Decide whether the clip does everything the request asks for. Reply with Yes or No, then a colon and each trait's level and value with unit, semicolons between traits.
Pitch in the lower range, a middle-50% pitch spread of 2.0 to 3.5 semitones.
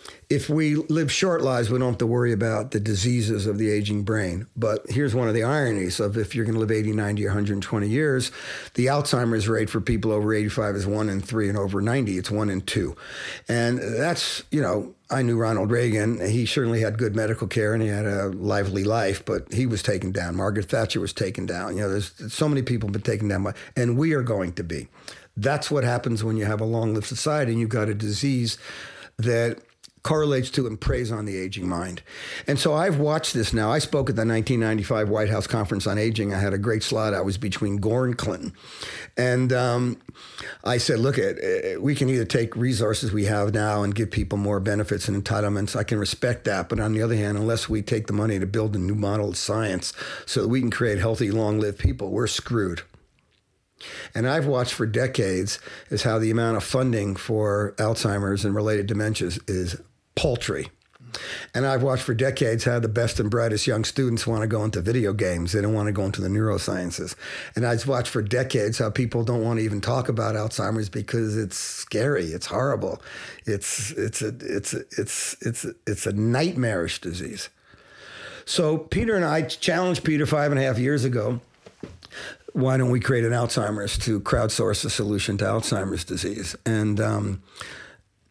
Yes: low, 110 Hz; average, 3.0 semitones